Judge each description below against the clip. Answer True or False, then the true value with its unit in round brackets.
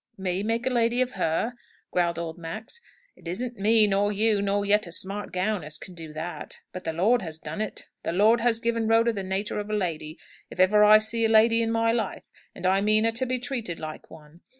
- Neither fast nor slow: False (235 wpm)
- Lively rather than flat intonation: False (4.1 semitones)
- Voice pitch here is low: False (210 Hz)